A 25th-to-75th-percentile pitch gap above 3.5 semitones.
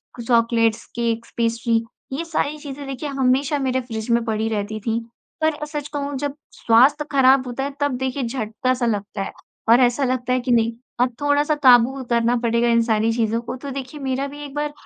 No: average, 3.2 semitones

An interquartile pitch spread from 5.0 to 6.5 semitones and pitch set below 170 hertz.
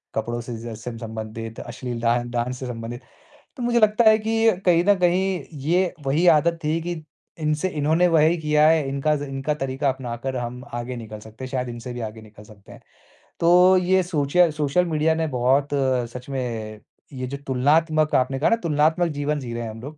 Yes: average, 5.3 semitones; medium, 140 Hz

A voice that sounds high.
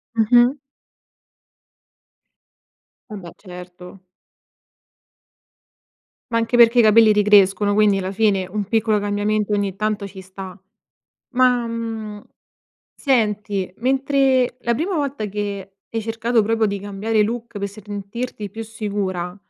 Yes: high, 210 Hz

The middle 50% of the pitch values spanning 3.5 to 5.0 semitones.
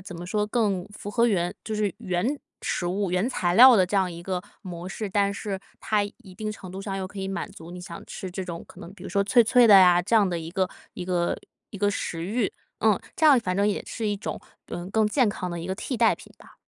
No: average, 2.9 semitones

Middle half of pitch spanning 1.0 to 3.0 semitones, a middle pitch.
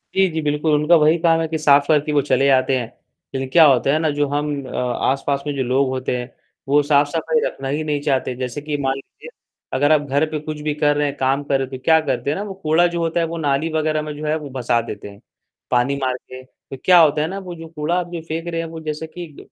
Yes: average, 2.7 semitones; medium, 150 Hz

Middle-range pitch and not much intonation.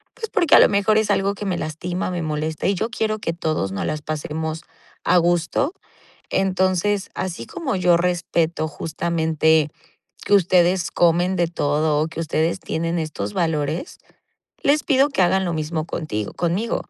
No: medium, 170 Hz; average, 3.3 semitones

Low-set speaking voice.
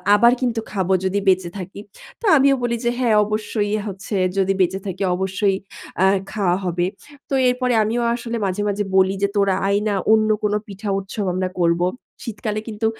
No: high, 205 Hz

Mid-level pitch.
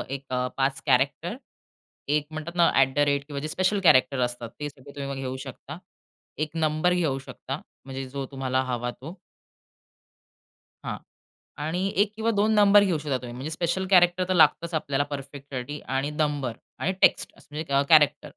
Yes: medium, 145 Hz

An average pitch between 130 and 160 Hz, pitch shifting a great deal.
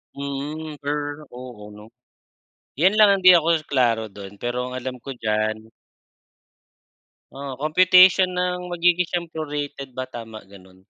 Yes: medium, 140 Hz; wide, 6.9 semitones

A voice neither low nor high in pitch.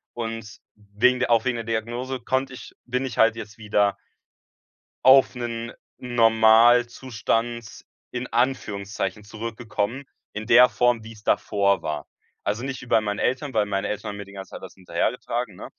No: low, 115 Hz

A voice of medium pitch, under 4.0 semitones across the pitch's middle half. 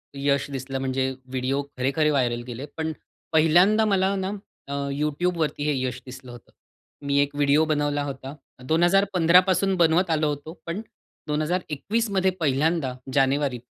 No: medium, 150 Hz; average, 4.3 semitones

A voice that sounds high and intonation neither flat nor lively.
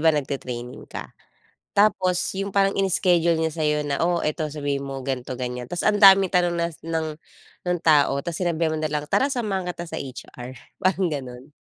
No: medium, 160 Hz; average, 4.4 semitones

